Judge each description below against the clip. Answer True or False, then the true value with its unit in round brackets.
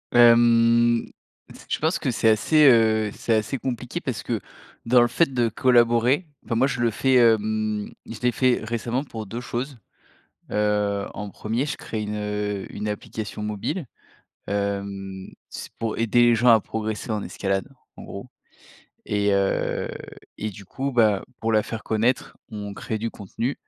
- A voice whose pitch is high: False (115 Hz)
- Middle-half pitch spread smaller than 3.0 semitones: True (2.5 semitones)